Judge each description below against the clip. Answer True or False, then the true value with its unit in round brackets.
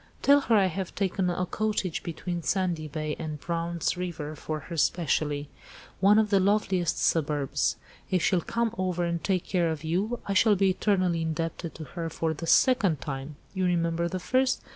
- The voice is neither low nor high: True (175 Hz)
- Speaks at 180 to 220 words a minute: True (185 wpm)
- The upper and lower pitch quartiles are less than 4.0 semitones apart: True (3.2 semitones)